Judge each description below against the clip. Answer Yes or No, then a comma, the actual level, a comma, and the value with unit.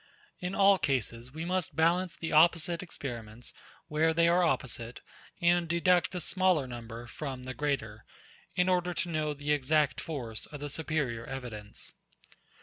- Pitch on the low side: No, medium, 150 Hz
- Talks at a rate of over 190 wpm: No, average, 150 wpm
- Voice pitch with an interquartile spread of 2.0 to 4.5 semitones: No, average, 5.3 semitones